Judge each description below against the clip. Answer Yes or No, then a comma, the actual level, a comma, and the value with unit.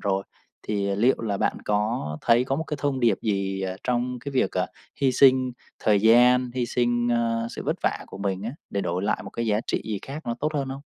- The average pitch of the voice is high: No, low, 115 Hz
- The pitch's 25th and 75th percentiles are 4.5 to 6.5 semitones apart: No, average, 4.0 semitones